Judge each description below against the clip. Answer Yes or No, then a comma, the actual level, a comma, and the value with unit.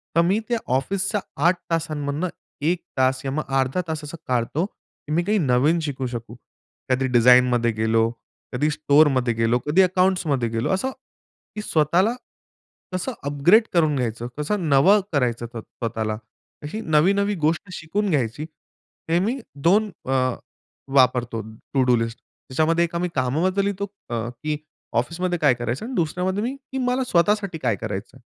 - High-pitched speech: No, medium, 150 Hz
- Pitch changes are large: Yes, wide, 6.6 semitones